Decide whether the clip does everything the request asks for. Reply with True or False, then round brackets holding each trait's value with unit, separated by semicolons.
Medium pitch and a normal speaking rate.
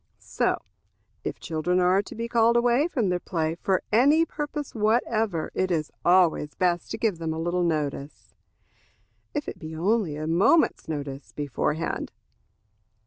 True (180 Hz; 150 wpm)